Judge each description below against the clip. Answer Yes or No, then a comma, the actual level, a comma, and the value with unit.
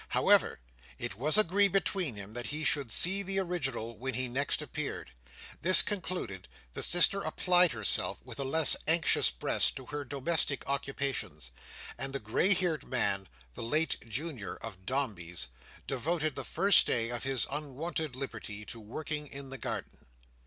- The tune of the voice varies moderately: No, wide, 6.0 semitones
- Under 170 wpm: Yes, average, 155 wpm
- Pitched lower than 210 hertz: Yes, medium, 140 Hz